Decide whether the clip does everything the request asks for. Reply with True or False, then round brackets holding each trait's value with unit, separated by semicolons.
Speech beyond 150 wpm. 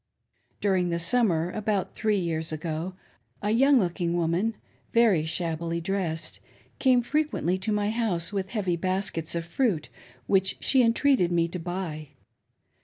False (140 wpm)